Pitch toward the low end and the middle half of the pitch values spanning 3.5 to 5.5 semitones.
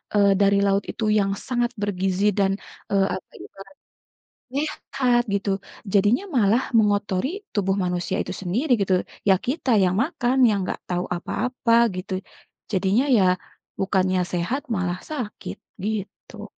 No: high, 200 Hz; average, 4.1 semitones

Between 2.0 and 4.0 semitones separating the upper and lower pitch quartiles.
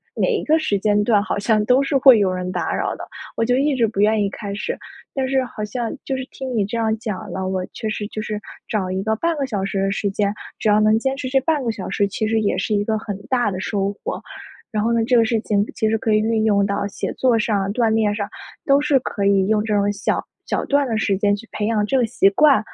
Yes: average, 3.0 semitones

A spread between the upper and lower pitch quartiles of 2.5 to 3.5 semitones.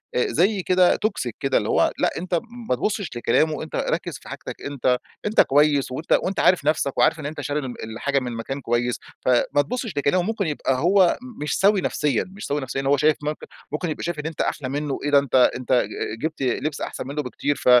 No: average, 4.4 semitones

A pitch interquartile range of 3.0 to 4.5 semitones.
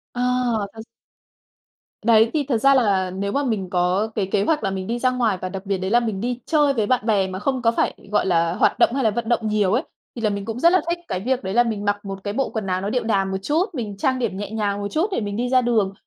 Yes: average, 3.9 semitones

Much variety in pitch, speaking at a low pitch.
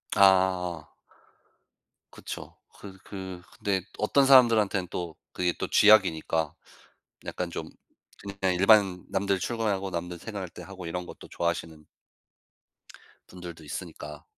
No: narrow, 2.6 semitones; very low, 95 Hz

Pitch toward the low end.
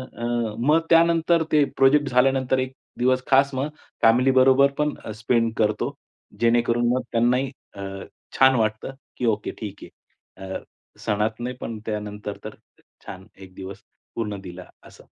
Yes: low, 120 Hz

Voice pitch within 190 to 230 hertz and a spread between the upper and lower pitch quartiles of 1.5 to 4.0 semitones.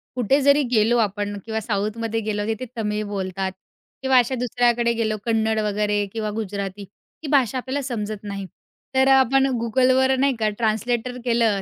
Yes: high, 225 Hz; average, 3.1 semitones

